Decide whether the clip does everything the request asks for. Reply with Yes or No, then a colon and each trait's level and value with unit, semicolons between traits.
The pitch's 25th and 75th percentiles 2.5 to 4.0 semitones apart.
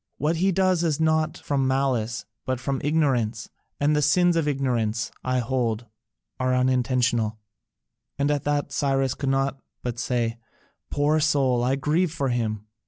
Yes: average, 3.3 semitones